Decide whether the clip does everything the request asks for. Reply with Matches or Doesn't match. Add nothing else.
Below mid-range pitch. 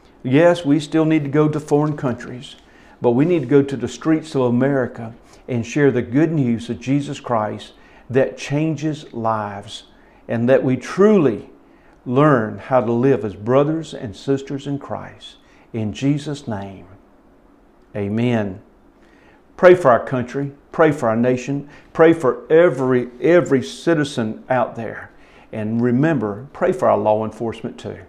Matches